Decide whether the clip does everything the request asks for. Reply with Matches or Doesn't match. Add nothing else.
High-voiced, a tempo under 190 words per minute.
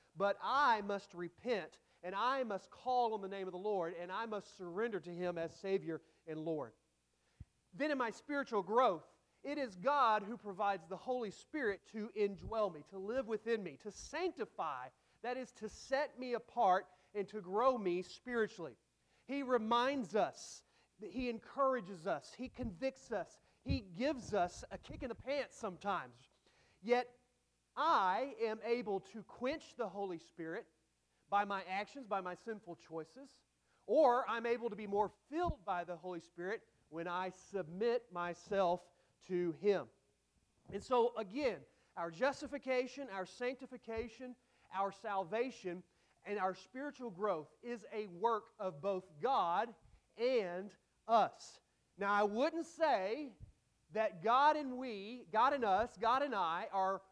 Matches